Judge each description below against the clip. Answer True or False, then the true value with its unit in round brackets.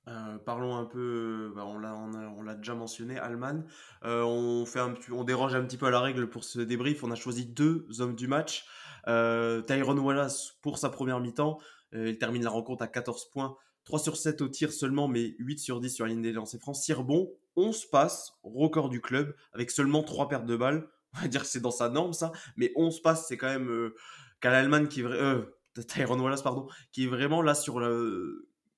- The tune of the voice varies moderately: True (3.6 semitones)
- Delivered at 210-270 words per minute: True (220 wpm)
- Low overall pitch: True (130 Hz)